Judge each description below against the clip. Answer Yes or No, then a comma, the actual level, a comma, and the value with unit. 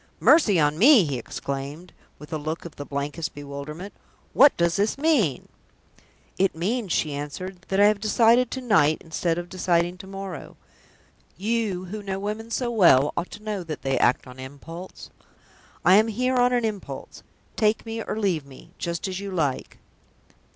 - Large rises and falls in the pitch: Yes, wide, 5.7 semitones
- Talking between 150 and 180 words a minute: Yes, average, 175 wpm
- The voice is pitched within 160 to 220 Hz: Yes, medium, 185 Hz